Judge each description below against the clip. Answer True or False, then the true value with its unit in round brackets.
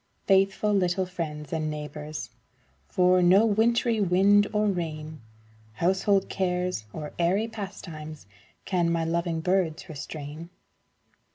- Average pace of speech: False (110 wpm)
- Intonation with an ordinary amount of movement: True (3.8 semitones)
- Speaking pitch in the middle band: True (180 Hz)